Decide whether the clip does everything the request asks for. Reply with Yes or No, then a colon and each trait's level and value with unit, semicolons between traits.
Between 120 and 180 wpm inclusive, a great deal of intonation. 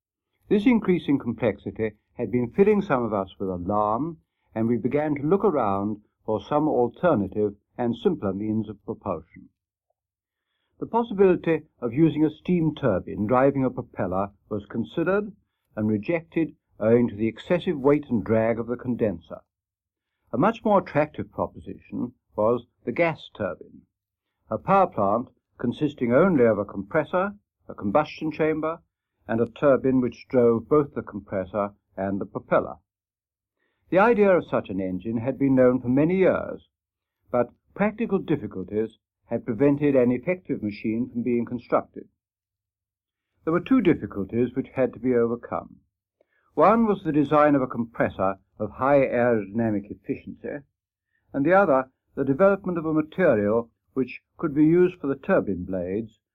Yes: average, 150 wpm; wide, 6.4 semitones